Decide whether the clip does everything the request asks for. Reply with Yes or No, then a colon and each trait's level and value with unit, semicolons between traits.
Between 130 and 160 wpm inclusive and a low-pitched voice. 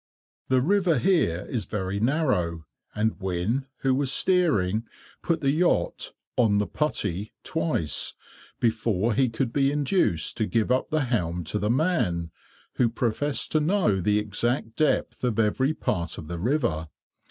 Yes: average, 155 wpm; low, 115 Hz